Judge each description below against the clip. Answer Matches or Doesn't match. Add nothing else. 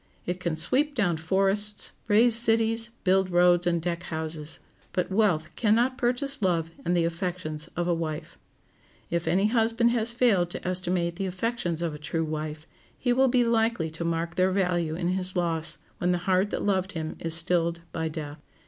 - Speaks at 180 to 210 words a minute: Matches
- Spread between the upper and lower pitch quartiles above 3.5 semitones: Matches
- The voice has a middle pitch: Matches